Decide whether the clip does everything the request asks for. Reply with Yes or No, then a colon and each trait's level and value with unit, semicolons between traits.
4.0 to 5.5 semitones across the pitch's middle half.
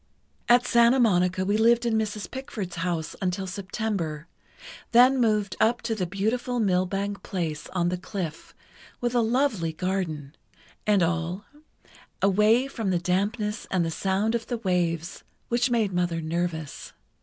Yes: average, 4.4 semitones